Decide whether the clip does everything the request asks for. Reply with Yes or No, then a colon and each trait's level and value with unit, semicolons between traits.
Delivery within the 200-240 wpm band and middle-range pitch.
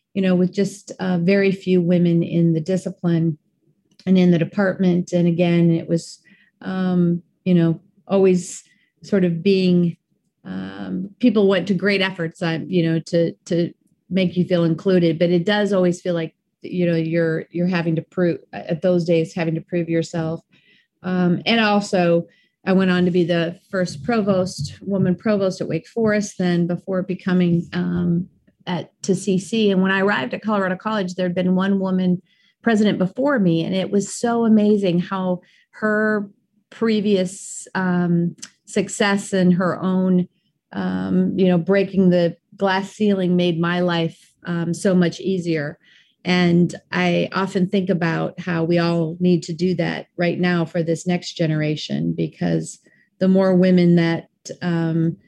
No: average, 160 wpm; medium, 180 Hz